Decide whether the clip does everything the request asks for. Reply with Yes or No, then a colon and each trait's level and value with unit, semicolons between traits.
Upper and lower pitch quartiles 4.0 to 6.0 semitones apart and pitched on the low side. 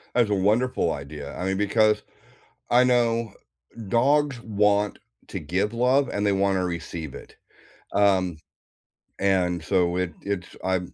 Yes: average, 4.3 semitones; low, 100 Hz